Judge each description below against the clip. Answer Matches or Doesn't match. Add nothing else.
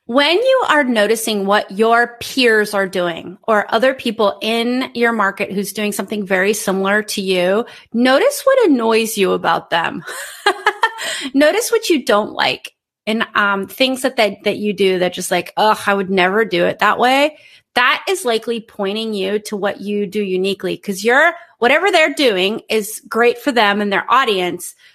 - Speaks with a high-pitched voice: Matches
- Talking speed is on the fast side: Doesn't match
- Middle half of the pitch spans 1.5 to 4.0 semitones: Doesn't match